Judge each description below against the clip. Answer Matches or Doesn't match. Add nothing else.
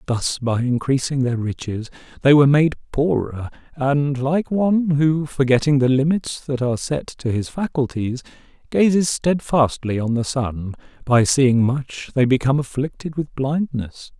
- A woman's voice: Doesn't match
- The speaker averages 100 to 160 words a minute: Matches